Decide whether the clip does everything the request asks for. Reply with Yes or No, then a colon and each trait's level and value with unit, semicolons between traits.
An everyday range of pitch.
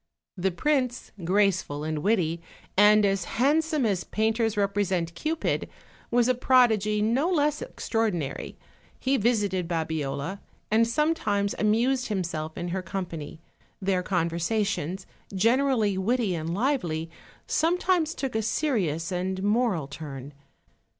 No: wide, 5.9 semitones